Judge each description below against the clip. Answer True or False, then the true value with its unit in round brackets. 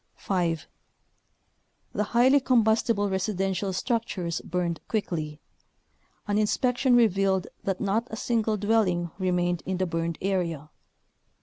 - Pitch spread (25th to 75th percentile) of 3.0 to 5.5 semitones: True (3.9 semitones)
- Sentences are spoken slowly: True (115 wpm)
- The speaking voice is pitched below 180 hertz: False (195 Hz)